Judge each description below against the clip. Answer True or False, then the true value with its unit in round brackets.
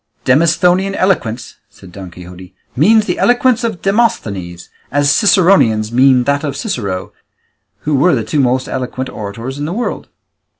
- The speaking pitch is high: False (140 Hz)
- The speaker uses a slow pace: False (145 wpm)